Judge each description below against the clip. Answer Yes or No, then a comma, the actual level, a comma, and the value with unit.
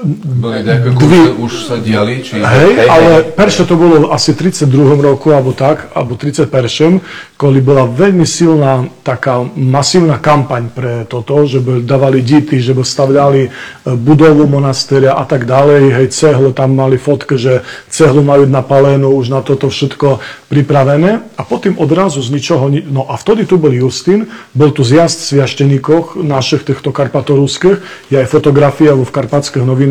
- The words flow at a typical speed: Yes, average, 155 wpm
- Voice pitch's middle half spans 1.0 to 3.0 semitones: Yes, narrow, 2.6 semitones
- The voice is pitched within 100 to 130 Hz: No, medium, 140 Hz